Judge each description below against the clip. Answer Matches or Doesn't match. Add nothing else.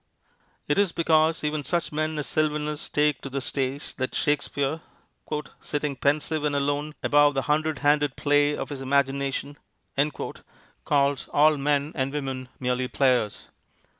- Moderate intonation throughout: Doesn't match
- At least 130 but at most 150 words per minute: Matches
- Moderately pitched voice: Matches